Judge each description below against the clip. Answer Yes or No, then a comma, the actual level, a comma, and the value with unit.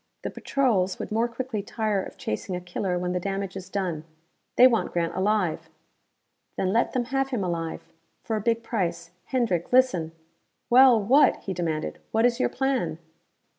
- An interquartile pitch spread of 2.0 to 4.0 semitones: No, average, 5.1 semitones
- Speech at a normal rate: Yes, average, 180 wpm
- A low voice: No, high, 200 Hz